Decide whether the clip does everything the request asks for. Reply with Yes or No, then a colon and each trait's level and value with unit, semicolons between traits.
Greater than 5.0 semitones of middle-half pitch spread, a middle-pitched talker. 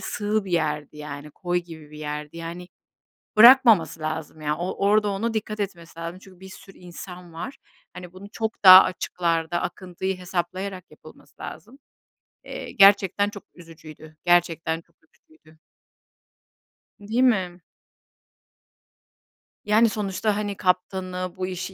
No: average, 3.3 semitones; medium, 180 Hz